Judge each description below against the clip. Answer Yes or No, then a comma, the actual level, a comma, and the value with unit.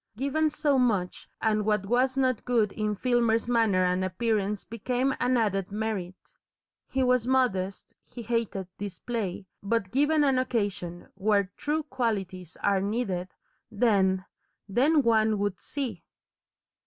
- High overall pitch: Yes, high, 220 Hz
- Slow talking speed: Yes, slow, 130 wpm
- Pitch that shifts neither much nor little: Yes, average, 4.2 semitones